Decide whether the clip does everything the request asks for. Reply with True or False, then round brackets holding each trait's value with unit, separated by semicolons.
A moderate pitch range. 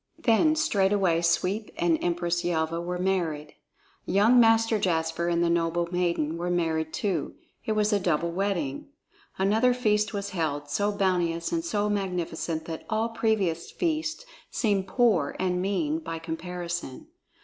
True (3.9 semitones)